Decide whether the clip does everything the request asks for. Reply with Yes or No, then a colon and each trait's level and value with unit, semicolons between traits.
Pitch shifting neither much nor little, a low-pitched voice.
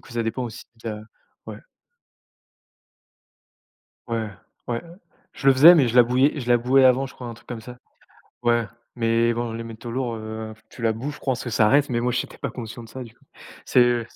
No: narrow, 1.9 semitones; low, 120 Hz